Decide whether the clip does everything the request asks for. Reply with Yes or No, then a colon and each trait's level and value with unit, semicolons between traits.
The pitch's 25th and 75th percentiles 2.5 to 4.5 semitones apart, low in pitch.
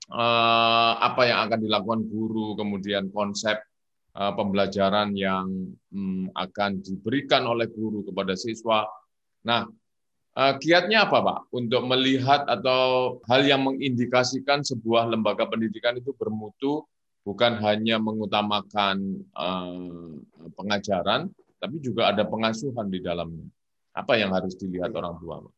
Yes: average, 3.8 semitones; low, 110 Hz